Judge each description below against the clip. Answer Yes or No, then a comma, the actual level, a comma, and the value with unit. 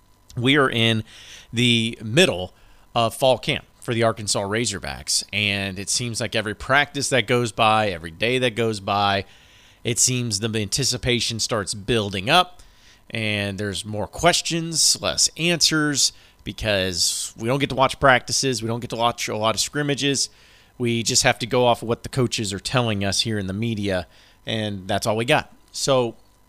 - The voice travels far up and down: No, average, 3.8 semitones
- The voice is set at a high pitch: No, low, 115 Hz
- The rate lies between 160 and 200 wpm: Yes, average, 175 wpm